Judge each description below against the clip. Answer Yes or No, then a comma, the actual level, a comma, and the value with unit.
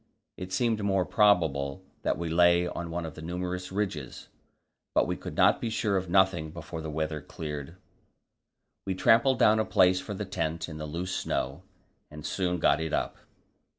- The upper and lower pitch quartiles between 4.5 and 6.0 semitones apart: No, average, 3.3 semitones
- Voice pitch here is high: No, very low, 90 Hz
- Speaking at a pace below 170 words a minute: No, average, 180 wpm